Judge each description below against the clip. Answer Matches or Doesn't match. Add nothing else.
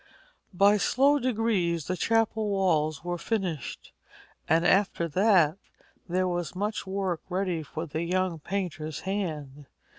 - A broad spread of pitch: Doesn't match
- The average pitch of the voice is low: Doesn't match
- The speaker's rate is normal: Doesn't match